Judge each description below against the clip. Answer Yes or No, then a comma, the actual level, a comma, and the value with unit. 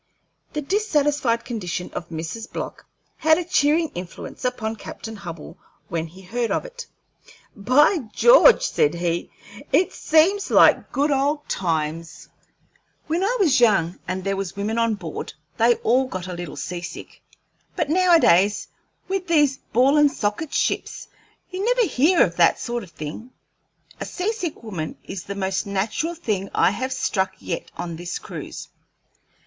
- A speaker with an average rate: Yes, average, 155 wpm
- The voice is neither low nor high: No, high, 230 Hz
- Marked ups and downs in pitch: Yes, wide, 9.0 semitones